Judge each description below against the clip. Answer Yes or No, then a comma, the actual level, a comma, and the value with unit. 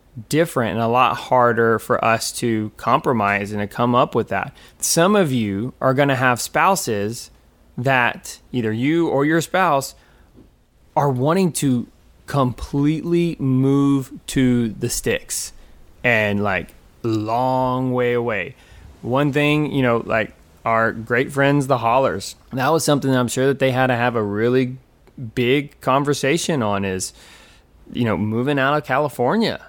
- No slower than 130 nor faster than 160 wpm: Yes, average, 150 wpm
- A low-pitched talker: Yes, low, 125 Hz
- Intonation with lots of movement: No, average, 3.4 semitones